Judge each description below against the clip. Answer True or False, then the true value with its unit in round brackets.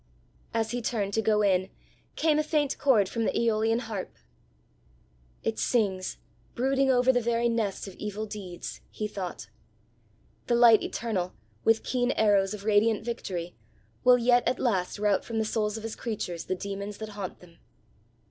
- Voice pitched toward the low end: False (220 Hz)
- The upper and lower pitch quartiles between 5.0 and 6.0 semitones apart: False (3.0 semitones)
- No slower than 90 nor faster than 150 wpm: False (165 wpm)